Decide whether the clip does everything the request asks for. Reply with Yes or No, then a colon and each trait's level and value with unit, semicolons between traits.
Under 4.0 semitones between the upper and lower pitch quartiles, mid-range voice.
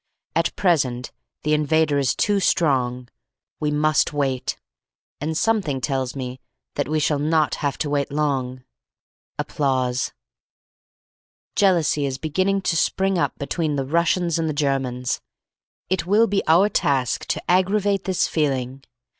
No: average, 4.3 semitones; medium, 150 Hz